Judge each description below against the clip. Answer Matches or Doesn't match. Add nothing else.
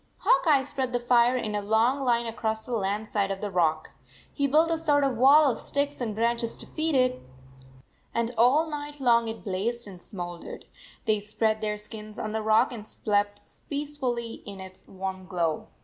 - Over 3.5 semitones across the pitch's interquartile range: Matches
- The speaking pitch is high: Matches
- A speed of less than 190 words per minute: Doesn't match